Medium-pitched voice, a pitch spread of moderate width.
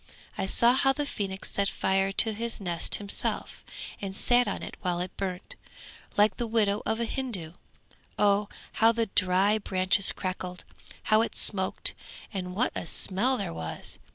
No: high, 200 Hz; average, 3.3 semitones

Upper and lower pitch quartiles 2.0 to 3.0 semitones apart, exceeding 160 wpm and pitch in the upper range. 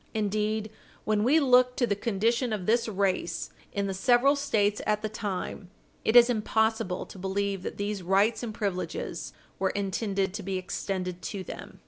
Yes: average, 2.7 semitones; average, 170 wpm; high, 210 Hz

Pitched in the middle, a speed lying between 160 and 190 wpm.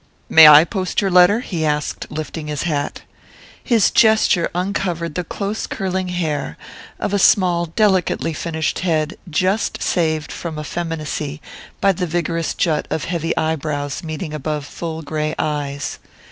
No: medium, 165 Hz; average, 145 wpm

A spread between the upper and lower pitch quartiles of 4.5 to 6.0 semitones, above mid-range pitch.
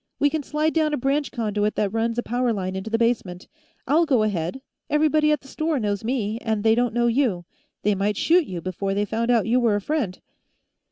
Yes: average, 5.3 semitones; high, 230 Hz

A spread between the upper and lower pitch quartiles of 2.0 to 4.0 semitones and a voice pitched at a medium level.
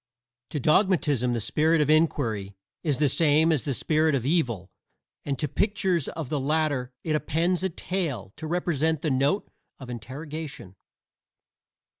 Yes: average, 3.7 semitones; medium, 150 Hz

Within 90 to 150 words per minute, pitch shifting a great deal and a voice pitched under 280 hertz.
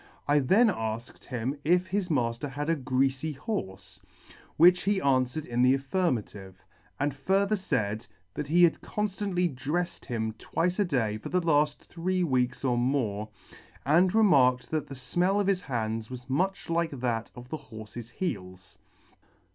No: average, 165 wpm; wide, 6.6 semitones; medium, 140 Hz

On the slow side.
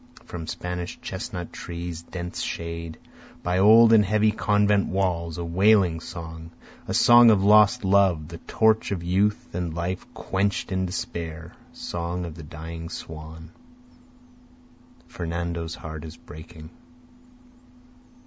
Yes: slow, 120 wpm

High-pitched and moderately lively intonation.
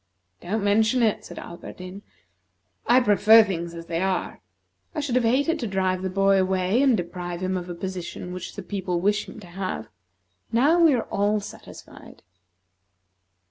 Yes: high, 195 Hz; average, 3.7 semitones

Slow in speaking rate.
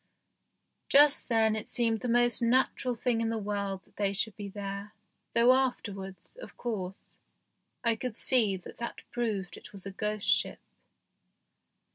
No: average, 155 wpm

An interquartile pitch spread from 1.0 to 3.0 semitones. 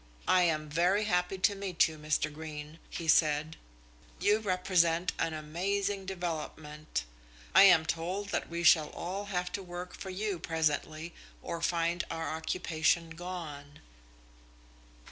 Yes: average, 2.7 semitones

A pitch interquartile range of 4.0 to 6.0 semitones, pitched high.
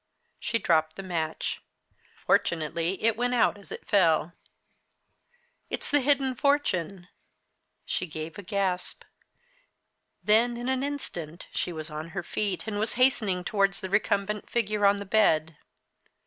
Yes: average, 5.1 semitones; high, 200 Hz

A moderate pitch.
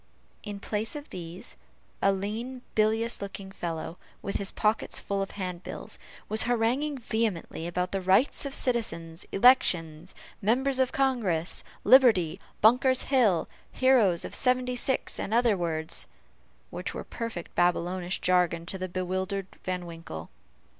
No: high, 200 Hz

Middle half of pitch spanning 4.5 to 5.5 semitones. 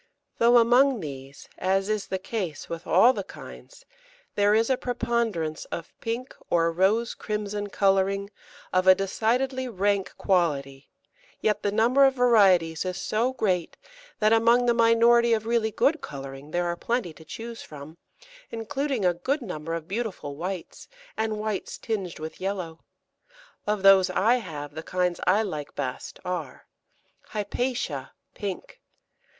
Yes: average, 5.1 semitones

